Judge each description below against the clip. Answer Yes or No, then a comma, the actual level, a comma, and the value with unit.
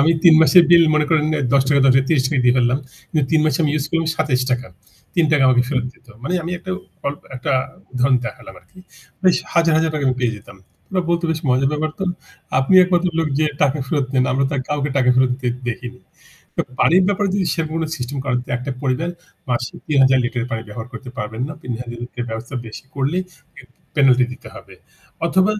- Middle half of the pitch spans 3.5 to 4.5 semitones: Yes, average, 4.1 semitones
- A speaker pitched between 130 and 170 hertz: Yes, low, 135 Hz